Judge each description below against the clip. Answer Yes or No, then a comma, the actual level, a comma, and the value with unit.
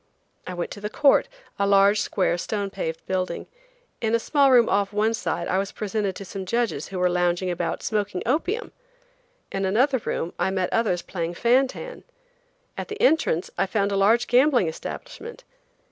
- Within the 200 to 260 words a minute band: No, average, 185 wpm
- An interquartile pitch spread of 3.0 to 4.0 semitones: No, average, 4.4 semitones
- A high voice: Yes, high, 200 Hz